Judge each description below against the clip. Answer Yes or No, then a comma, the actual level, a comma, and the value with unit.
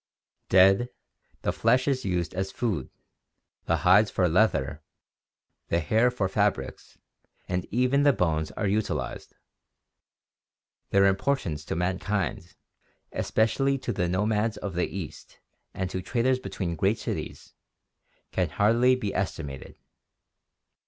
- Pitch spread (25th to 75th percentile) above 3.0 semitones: Yes, average, 4.3 semitones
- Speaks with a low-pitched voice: Yes, low, 100 Hz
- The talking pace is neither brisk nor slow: No, slow, 120 wpm